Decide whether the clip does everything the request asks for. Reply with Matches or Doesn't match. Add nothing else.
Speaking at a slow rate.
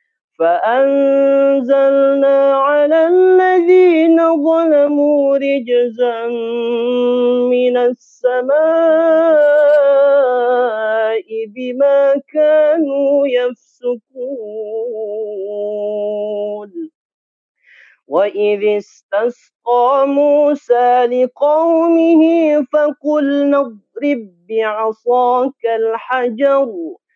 Matches